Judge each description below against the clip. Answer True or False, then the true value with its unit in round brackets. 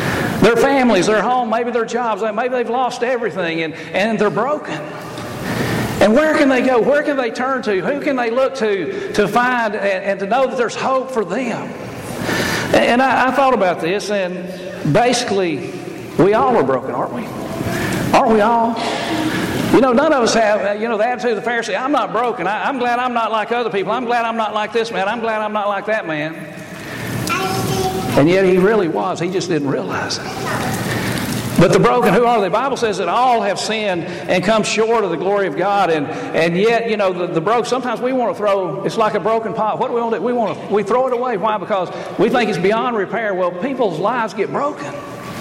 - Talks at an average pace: False (225 wpm)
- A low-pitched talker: False (220 Hz)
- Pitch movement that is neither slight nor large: True (3.8 semitones)